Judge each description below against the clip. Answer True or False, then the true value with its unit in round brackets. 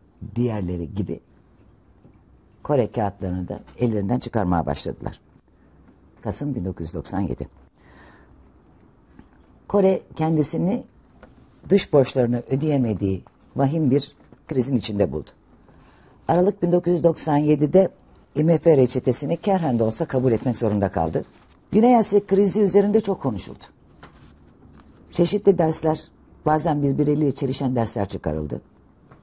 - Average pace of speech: False (90 wpm)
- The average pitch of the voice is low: True (130 Hz)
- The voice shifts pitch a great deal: True (8.6 semitones)